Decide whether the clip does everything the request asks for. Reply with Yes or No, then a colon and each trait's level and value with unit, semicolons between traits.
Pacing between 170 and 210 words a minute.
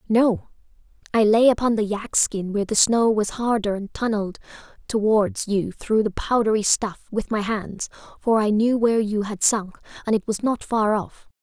Yes: average, 190 wpm